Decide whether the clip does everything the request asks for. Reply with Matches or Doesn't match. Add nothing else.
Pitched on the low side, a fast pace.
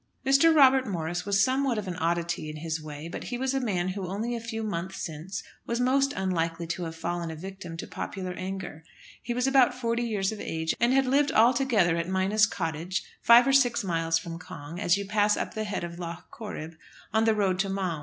Doesn't match